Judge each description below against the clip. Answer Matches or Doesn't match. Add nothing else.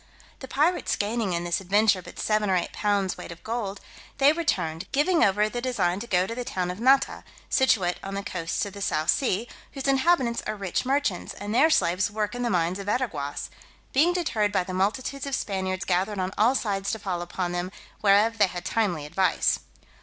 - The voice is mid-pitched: Doesn't match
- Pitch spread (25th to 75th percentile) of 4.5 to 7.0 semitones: Matches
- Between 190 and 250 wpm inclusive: Matches